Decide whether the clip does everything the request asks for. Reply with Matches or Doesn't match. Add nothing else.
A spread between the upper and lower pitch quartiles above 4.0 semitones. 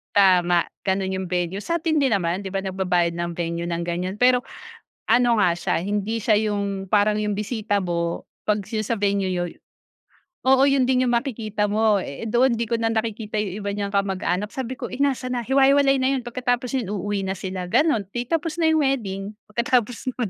Matches